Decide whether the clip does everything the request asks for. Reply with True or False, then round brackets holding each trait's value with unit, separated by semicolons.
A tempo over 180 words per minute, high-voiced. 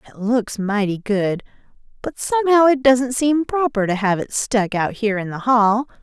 True (190 wpm; 230 Hz)